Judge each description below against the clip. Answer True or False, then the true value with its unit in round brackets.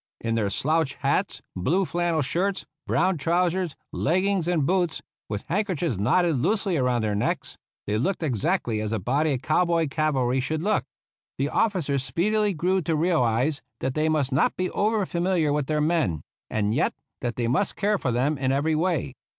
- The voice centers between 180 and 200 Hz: False (155 Hz)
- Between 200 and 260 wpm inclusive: False (180 wpm)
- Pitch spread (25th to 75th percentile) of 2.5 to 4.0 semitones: False (5.6 semitones)